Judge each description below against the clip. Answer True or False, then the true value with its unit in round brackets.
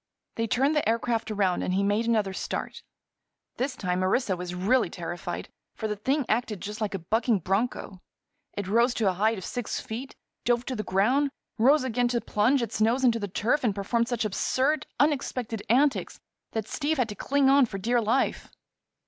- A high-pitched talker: True (230 Hz)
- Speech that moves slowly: False (190 wpm)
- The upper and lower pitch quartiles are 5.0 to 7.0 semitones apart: False (3.8 semitones)